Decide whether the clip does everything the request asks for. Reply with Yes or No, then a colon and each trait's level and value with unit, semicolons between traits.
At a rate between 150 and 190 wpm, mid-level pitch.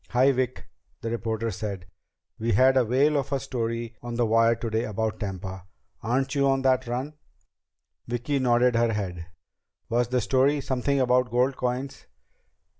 No: average, 160 wpm; low, 120 Hz